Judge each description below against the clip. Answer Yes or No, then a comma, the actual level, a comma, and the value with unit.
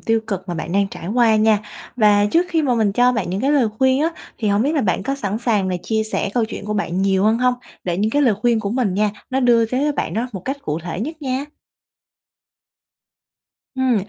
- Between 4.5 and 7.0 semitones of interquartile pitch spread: No, average, 4.1 semitones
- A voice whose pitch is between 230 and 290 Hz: No, high, 220 Hz